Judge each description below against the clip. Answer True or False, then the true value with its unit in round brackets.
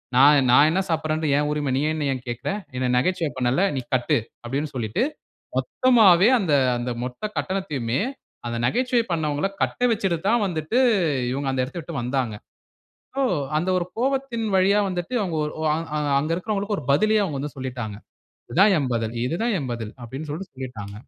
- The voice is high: False (155 Hz)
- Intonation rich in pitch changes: True (7.0 semitones)